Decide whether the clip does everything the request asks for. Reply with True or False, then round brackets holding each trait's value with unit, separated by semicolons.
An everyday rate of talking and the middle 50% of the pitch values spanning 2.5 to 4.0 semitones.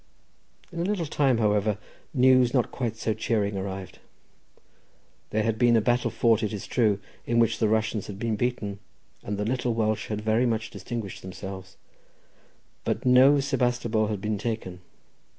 True (165 wpm; 2.8 semitones)